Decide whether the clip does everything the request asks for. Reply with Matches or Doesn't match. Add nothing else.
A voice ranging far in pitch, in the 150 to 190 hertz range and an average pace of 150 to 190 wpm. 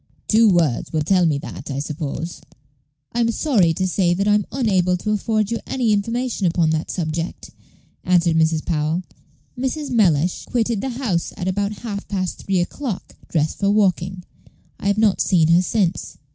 Doesn't match